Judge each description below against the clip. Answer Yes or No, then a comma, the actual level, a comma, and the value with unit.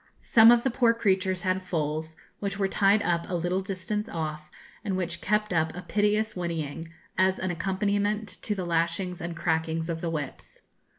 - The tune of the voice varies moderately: Yes, average, 3.6 semitones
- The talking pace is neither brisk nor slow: Yes, average, 180 wpm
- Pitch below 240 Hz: Yes, medium, 185 Hz